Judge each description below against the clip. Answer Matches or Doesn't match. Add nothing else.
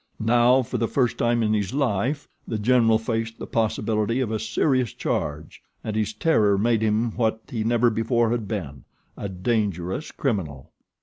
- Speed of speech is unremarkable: Matches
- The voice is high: Doesn't match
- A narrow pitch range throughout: Matches